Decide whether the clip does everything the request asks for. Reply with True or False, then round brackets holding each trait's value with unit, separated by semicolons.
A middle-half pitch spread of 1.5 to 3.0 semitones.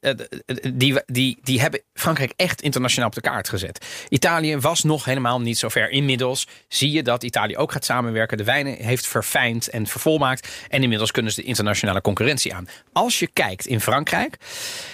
False (4.0 semitones)